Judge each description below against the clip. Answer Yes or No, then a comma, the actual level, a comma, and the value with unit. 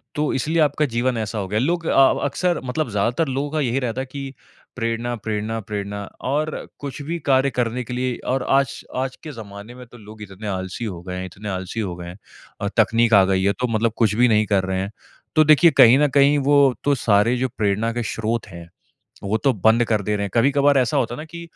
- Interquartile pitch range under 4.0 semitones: No, average, 4.7 semitones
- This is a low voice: Yes, low, 115 Hz